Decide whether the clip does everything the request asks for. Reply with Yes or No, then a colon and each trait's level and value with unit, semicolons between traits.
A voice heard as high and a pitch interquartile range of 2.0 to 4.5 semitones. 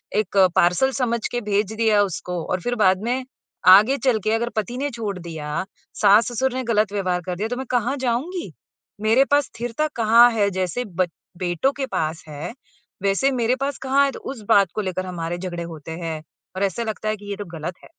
No: high, 215 Hz; average, 4.9 semitones